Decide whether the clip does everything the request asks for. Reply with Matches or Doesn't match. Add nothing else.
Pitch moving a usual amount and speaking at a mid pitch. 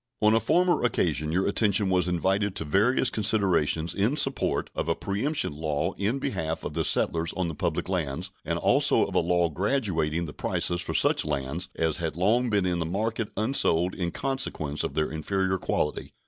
Doesn't match